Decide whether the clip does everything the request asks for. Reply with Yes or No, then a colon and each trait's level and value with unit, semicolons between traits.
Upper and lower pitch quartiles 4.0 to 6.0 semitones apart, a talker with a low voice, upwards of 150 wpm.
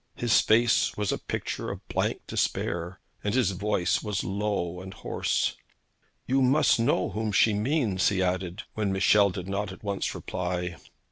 No: average, 2.8 semitones; low, 100 Hz; average, 160 wpm